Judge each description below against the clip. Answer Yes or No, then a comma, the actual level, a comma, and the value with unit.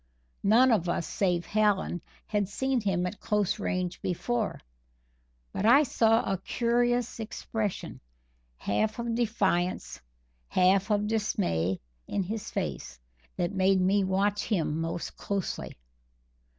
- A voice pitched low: No, high, 200 Hz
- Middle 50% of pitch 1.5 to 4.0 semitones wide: Yes, average, 3.5 semitones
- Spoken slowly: Yes, slow, 125 wpm